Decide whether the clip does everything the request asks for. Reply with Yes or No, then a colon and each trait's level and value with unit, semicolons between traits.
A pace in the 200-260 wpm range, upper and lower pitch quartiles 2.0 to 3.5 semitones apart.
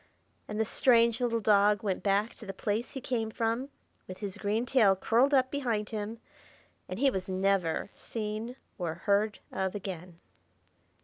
No: average, 165 wpm; average, 2.9 semitones